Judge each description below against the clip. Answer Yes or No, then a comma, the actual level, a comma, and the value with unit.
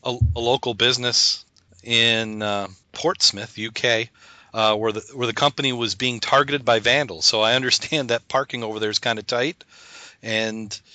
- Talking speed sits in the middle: Yes, average, 170 wpm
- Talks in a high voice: No, low, 115 Hz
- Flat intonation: Yes, narrow, 2.3 semitones